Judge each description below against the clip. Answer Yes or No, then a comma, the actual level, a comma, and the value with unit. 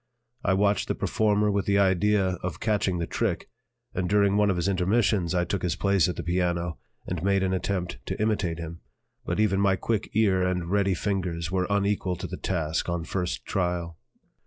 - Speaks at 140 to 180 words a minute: No, average, 195 wpm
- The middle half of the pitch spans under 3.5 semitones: Yes, narrow, 2.4 semitones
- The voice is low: Yes, very low, 95 Hz